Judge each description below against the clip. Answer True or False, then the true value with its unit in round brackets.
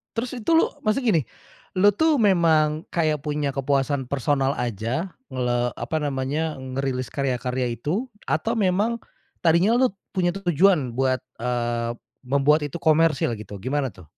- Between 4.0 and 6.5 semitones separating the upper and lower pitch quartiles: True (5.3 semitones)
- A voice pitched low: False (145 Hz)